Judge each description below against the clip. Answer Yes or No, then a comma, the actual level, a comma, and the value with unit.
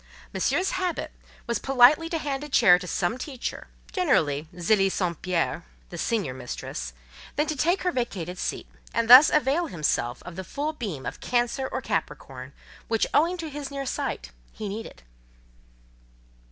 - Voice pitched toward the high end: Yes, high, 235 Hz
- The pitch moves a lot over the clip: Yes, wide, 8.8 semitones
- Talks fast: No, average, 160 wpm